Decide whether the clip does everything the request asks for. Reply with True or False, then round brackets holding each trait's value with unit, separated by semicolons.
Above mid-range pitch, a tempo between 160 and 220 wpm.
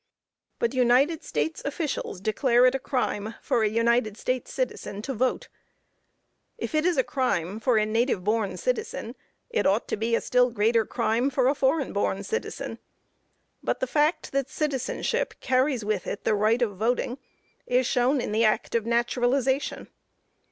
True (245 Hz; 165 wpm)